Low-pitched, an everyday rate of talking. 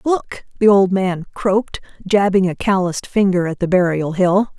No: high, 190 Hz; average, 170 wpm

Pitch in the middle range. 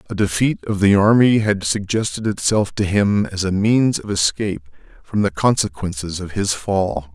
No: low, 100 Hz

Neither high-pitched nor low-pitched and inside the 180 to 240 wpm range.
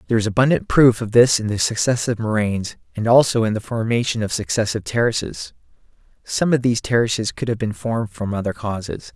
No: low, 110 Hz; average, 190 wpm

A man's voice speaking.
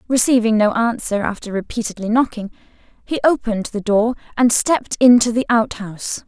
No: female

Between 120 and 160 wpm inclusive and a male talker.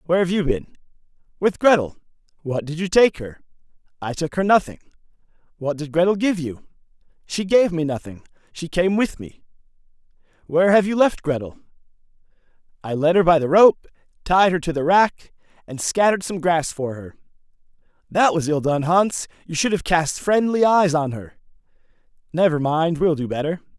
No: average, 170 wpm; male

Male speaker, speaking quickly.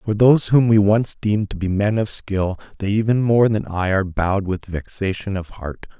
Yes: male; fast, 220 wpm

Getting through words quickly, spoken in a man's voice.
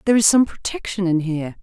No: fast, 220 wpm; female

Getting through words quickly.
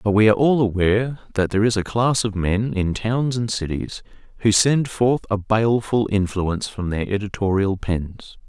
No: average, 185 wpm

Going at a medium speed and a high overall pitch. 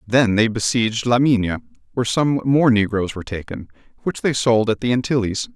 No: average, 185 wpm; low, 115 Hz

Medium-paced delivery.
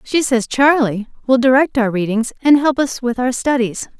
Yes: average, 195 wpm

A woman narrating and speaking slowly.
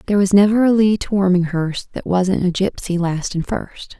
No: female; fast, 210 wpm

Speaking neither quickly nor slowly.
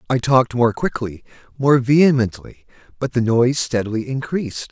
No: slow, 125 wpm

